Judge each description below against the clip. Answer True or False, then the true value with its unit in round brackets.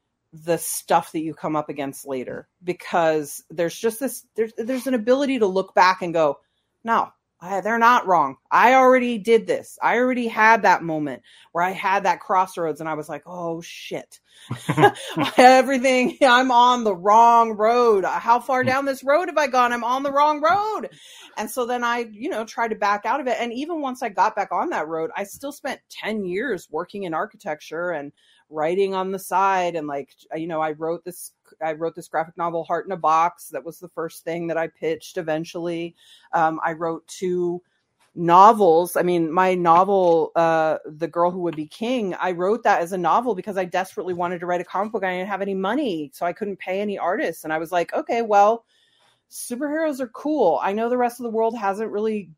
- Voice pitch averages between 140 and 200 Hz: True (190 Hz)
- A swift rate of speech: True (210 wpm)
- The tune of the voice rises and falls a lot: True (5.9 semitones)